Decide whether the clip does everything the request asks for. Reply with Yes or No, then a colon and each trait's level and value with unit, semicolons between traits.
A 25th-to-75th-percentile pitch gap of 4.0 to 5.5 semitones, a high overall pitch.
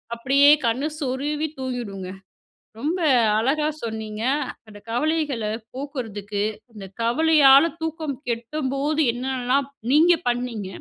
Yes: average, 4.5 semitones; very high, 260 Hz